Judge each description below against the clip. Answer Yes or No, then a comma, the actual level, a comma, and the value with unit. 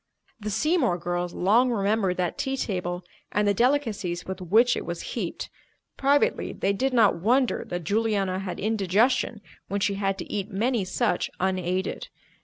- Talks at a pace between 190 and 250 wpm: No, average, 160 wpm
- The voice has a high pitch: Yes, high, 200 Hz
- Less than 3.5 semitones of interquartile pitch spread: No, average, 4.2 semitones